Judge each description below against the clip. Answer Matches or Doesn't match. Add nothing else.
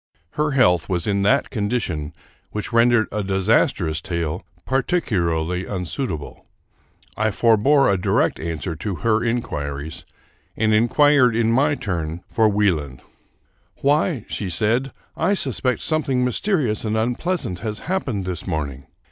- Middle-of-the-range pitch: Doesn't match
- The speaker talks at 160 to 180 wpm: Doesn't match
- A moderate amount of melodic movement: Doesn't match